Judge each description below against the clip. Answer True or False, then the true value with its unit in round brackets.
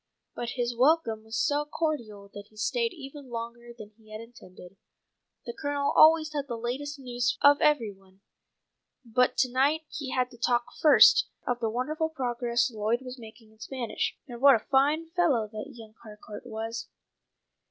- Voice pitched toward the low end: False (245 Hz)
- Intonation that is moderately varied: True (4.2 semitones)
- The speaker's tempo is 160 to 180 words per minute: True (175 wpm)